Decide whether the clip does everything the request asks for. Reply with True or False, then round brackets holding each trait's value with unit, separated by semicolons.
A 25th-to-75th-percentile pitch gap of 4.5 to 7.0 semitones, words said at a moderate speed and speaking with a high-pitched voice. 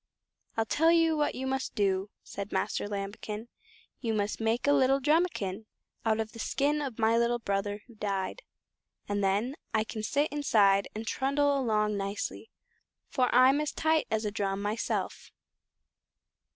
True (5.0 semitones; 160 wpm; 225 Hz)